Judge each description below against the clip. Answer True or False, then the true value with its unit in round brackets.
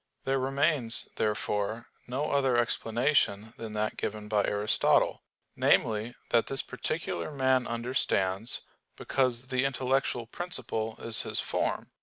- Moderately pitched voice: False (120 Hz)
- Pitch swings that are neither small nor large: True (3.4 semitones)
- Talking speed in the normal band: False (120 wpm)